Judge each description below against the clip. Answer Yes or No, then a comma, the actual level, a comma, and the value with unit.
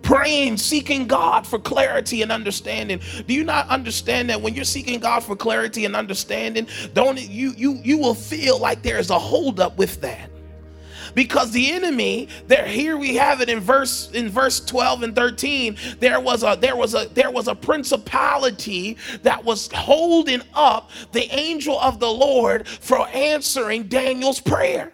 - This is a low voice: No, very high, 260 Hz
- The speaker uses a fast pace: No, average, 175 wpm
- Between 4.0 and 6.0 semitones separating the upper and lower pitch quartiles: No, average, 3.3 semitones